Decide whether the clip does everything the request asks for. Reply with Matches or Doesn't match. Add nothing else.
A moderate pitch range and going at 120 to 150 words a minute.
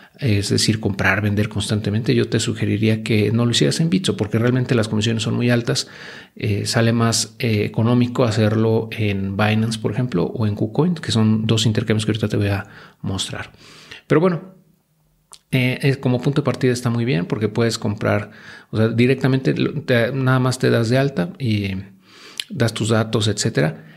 Doesn't match